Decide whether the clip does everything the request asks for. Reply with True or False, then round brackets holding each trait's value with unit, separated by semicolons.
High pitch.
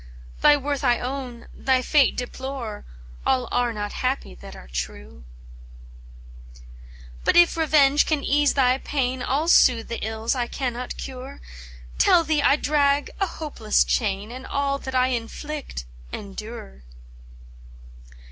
True (255 Hz)